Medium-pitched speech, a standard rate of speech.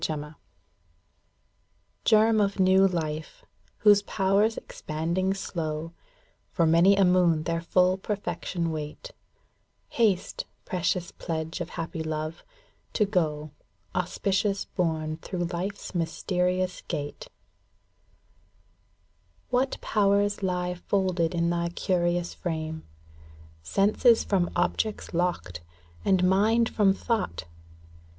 No: medium, 180 Hz; slow, 100 wpm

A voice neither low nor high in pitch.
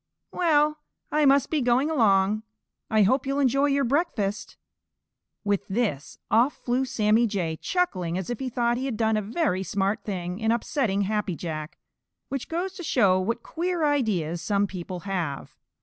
No: high, 225 Hz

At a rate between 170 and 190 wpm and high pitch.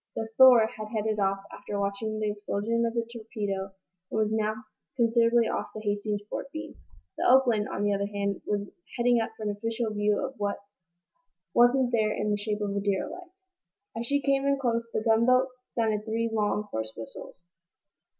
Yes: average, 185 wpm; high, 220 Hz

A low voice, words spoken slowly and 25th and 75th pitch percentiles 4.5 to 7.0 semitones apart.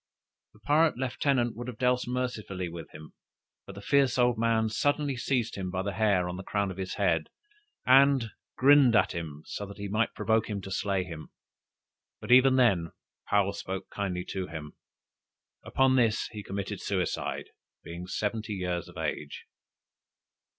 No: low, 105 Hz; average, 165 wpm; average, 5.1 semitones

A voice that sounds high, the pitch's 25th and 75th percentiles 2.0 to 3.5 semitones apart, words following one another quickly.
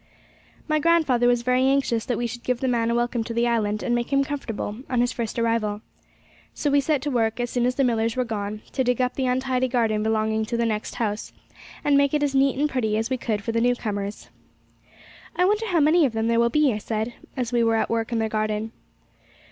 Yes: high, 240 Hz; average, 2.8 semitones; fast, 245 wpm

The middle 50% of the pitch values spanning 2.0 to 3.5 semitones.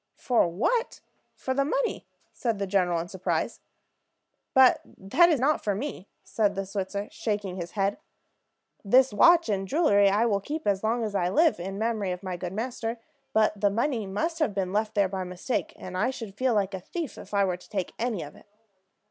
No: average, 4.6 semitones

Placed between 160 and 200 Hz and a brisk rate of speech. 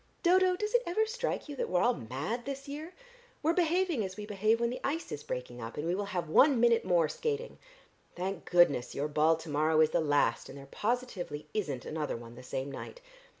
Yes: high, 190 Hz; fast, 220 wpm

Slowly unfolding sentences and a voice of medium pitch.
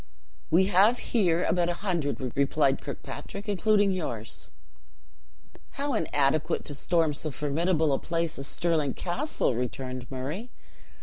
Yes: slow, 125 wpm; medium, 165 Hz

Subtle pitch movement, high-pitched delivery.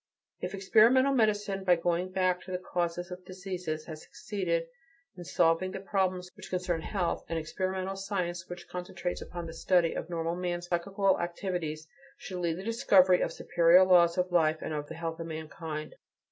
No: narrow, 2.1 semitones; medium, 180 Hz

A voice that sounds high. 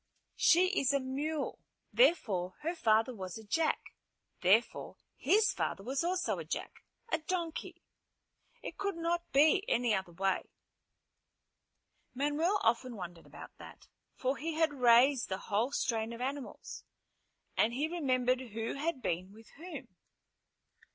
Yes: very high, 260 Hz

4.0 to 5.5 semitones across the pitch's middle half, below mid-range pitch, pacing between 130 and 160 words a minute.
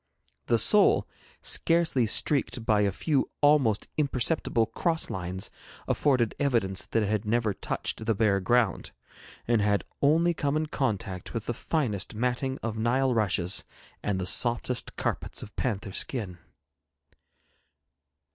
Yes: average, 4.6 semitones; low, 115 Hz; slow, 135 wpm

